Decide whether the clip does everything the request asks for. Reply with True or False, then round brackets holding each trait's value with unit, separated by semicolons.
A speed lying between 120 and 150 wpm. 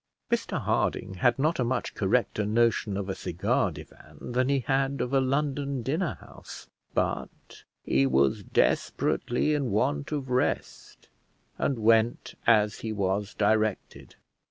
True (140 wpm)